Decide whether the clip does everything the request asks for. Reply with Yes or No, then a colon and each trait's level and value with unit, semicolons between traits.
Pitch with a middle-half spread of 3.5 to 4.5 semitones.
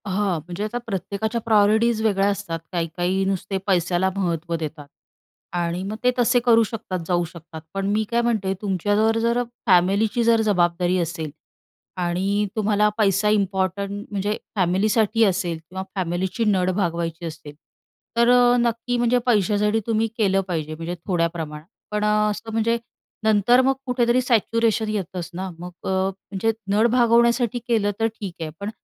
Yes: average, 4.0 semitones